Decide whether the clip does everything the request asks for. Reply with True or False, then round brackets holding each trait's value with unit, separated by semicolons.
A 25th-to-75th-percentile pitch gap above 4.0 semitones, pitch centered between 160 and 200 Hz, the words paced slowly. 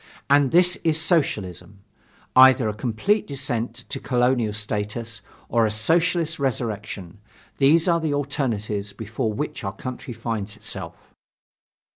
False (5.2 semitones; 120 Hz; 125 wpm)